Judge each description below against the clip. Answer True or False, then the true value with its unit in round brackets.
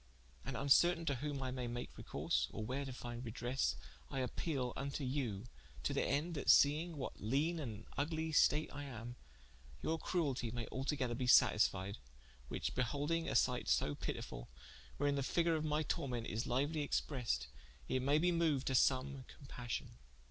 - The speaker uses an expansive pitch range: False (3.6 semitones)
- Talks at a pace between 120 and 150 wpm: False (170 wpm)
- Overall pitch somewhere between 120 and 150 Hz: True (135 Hz)